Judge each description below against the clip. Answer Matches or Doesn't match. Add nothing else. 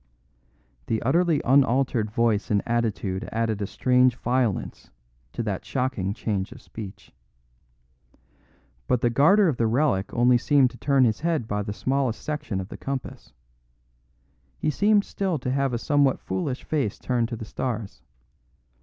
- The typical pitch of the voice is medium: Doesn't match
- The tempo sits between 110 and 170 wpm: Matches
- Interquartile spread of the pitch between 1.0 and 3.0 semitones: Doesn't match